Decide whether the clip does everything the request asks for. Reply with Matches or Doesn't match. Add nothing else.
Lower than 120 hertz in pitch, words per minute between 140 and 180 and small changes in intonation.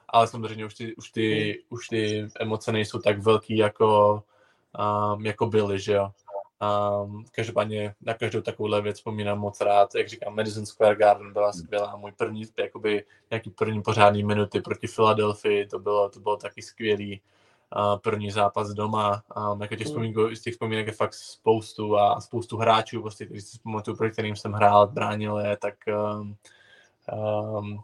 Matches